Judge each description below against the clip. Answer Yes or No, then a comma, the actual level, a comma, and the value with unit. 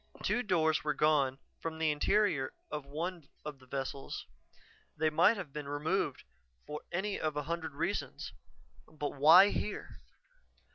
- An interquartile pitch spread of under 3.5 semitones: Yes, average, 3.0 semitones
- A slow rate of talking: No, average, 145 wpm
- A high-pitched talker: No, medium, 155 Hz